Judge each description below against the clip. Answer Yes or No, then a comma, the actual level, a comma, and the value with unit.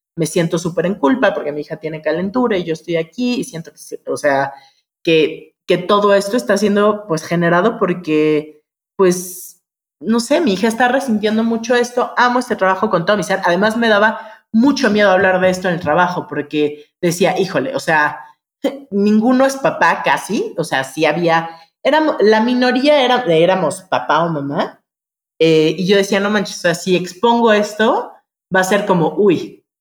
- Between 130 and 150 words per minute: No, average, 185 wpm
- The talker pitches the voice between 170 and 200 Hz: Yes, high, 190 Hz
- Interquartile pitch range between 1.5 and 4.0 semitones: No, wide, 5.5 semitones